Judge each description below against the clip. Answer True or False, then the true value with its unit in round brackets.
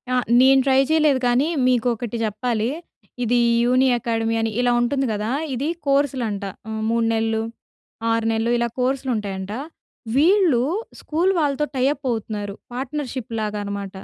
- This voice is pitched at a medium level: False (240 Hz)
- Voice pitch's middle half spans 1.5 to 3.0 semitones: False (3.4 semitones)